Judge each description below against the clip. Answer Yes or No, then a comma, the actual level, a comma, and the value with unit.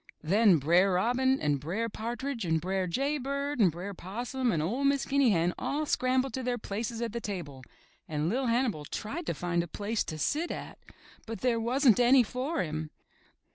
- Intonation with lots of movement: Yes, wide, 6.7 semitones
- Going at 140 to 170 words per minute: No, average, 190 wpm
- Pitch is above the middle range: Yes, high, 225 Hz